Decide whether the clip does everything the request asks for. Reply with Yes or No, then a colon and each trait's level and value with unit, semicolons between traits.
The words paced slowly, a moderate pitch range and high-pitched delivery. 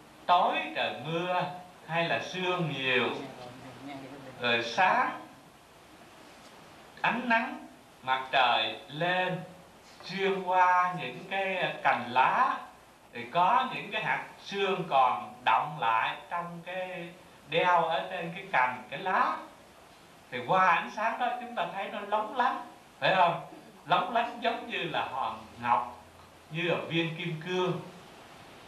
No: slow, 130 wpm; average, 3.8 semitones; medium, 180 Hz